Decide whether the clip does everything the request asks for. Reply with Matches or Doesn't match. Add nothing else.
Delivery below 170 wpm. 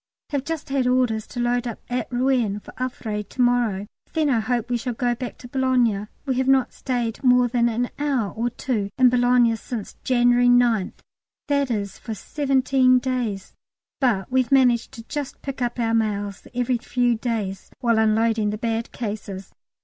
Doesn't match